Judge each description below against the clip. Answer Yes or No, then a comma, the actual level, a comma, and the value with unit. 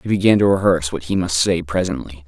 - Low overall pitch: Yes, very low, 85 Hz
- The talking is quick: Yes, fast, 235 wpm